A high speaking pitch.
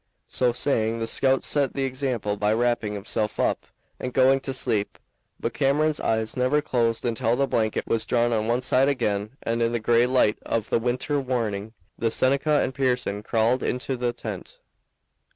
No: low, 120 Hz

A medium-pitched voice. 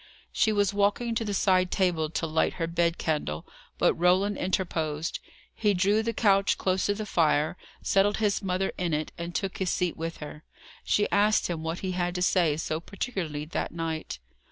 Yes: medium, 180 Hz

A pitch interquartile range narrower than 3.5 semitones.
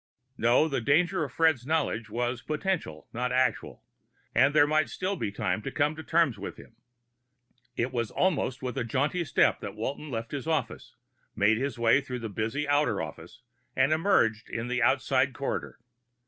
No: average, 4.7 semitones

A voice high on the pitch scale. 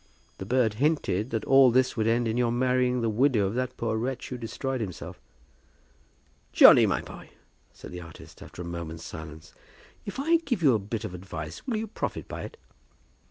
No: low, 115 Hz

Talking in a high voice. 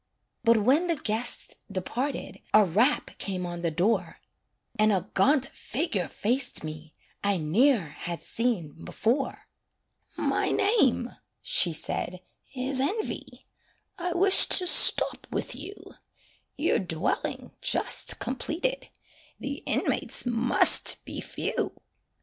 Yes: high, 230 Hz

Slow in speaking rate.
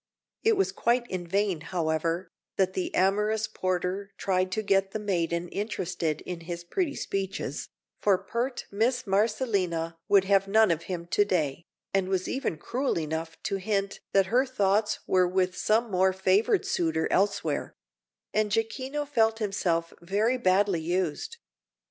No: average, 150 wpm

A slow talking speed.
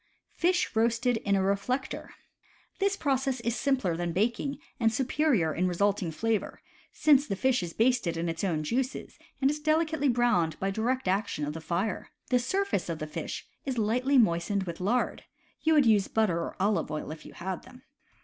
No: average, 190 wpm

